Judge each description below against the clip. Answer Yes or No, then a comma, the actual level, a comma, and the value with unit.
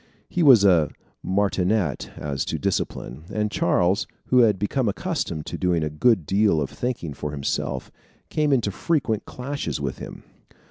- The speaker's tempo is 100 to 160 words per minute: Yes, average, 155 wpm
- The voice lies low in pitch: Yes, low, 100 Hz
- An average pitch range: No, wide, 7.8 semitones